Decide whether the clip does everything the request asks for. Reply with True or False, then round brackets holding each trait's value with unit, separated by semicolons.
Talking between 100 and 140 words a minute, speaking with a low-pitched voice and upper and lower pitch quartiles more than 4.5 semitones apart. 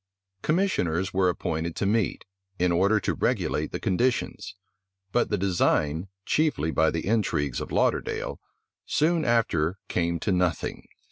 True (135 wpm; 95 Hz; 5.3 semitones)